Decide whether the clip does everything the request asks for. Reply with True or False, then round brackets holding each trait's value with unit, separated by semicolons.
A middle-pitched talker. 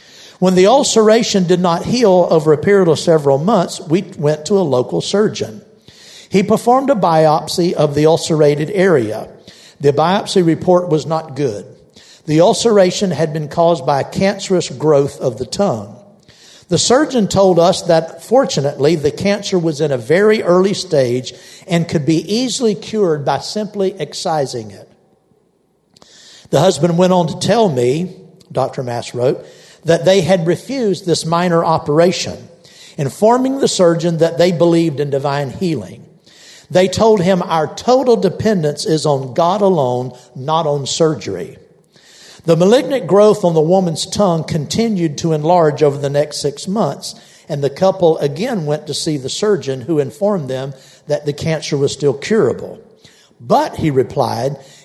True (170 Hz)